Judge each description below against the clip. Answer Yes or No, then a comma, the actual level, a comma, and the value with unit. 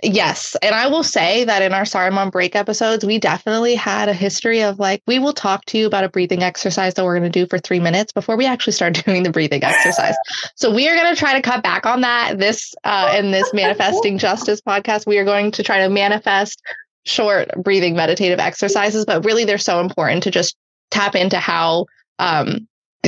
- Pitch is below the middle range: No, high, 200 Hz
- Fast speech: Yes, fast, 215 wpm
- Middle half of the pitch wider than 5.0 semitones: No, average, 3.1 semitones